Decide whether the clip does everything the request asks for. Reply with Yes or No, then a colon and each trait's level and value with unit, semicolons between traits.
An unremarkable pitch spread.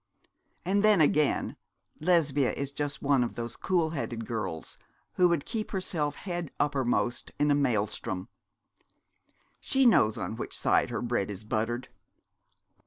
No: wide, 6.2 semitones